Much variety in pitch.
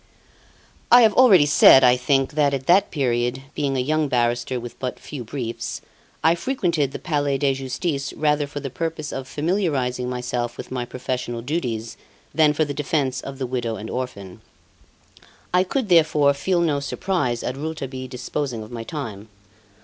No: average, 3.8 semitones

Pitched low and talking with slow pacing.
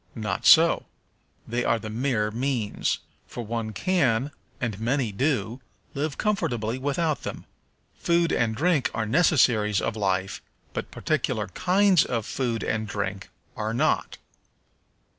Yes: low, 120 Hz; slow, 130 wpm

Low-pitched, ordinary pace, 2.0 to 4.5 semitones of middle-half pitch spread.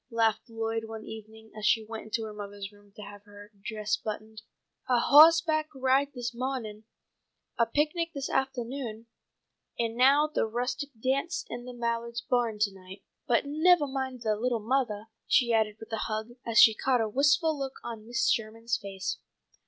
No: high, 230 Hz; average, 175 wpm; average, 3.5 semitones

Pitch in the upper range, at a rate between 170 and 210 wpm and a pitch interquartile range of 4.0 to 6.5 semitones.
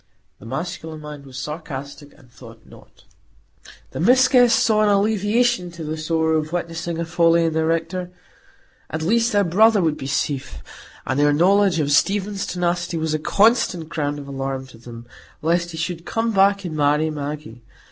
No: medium, 165 Hz; average, 180 wpm; average, 4.6 semitones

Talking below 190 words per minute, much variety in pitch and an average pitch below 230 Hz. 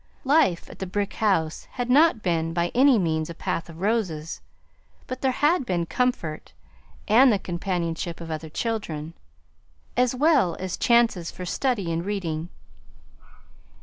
Yes: average, 150 wpm; wide, 6.6 semitones; medium, 185 Hz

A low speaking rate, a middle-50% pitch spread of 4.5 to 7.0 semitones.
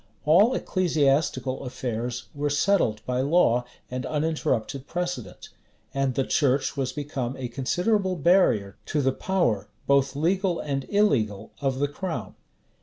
Yes: slow, 130 wpm; average, 5.2 semitones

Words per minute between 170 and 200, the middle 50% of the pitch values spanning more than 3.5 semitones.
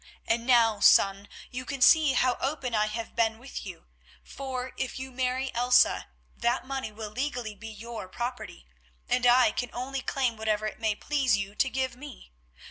No: average, 180 wpm; average, 2.9 semitones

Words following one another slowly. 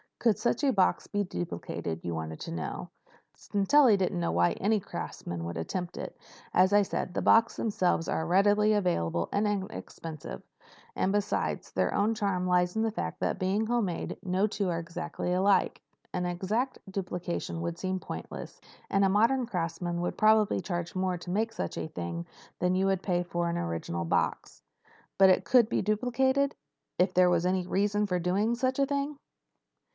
No: average, 175 wpm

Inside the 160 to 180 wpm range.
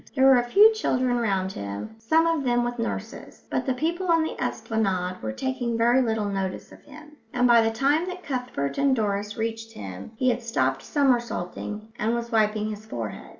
No: average, 195 wpm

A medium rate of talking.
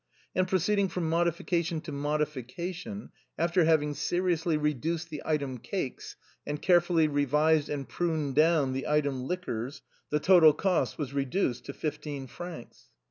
Yes: average, 150 wpm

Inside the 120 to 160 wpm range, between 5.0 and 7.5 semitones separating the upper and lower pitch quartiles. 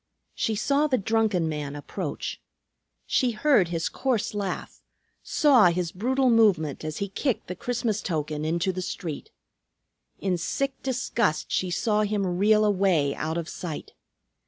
Yes: average, 145 wpm; wide, 5.4 semitones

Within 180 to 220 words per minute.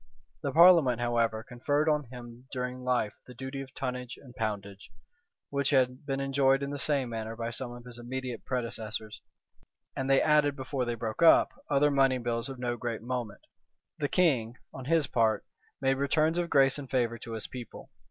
Yes: average, 185 wpm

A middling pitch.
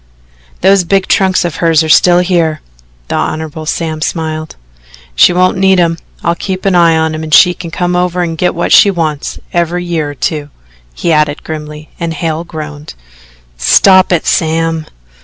Yes: medium, 165 Hz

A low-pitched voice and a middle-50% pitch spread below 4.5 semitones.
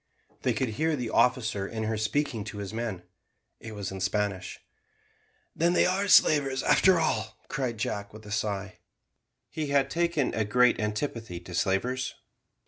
No: low, 115 Hz; average, 5.3 semitones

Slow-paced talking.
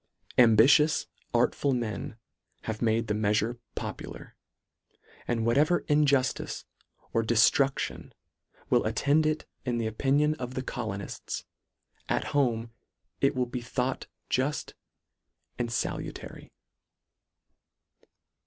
Yes: slow, 100 wpm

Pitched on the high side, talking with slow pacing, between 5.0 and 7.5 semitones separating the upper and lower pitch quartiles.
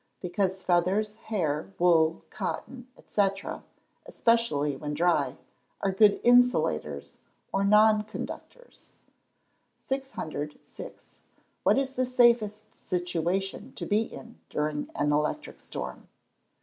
Yes: high, 195 Hz; slow, 105 wpm; wide, 5.6 semitones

